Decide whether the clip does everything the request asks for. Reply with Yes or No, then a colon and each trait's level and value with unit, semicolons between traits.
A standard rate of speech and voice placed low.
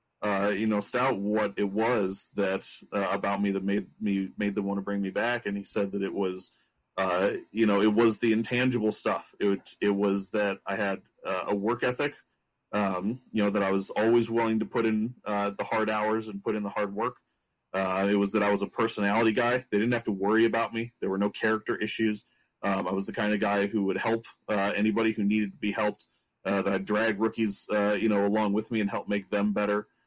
No: fast, 240 wpm; low, 105 Hz